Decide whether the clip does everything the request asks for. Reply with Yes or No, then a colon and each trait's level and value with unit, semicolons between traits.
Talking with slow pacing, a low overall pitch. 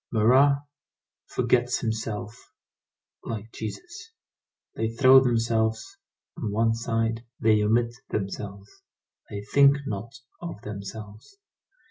Yes: slow, 95 wpm; low, 115 Hz